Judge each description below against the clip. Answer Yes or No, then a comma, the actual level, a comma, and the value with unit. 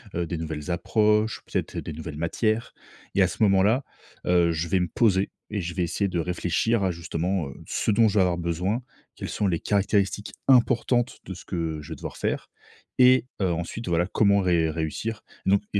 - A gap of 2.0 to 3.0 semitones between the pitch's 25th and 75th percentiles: No, average, 4.0 semitones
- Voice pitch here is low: Yes, very low, 95 Hz